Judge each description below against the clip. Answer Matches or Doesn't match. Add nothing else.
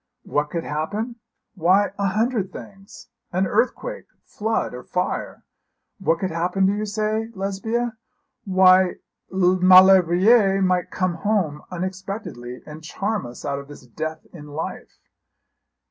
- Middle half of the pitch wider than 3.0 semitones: Matches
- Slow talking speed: Matches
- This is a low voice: Doesn't match